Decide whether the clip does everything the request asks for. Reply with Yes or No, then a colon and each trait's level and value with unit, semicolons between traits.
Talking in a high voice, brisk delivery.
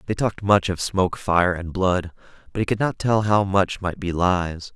No: very low, 95 Hz; fast, 225 wpm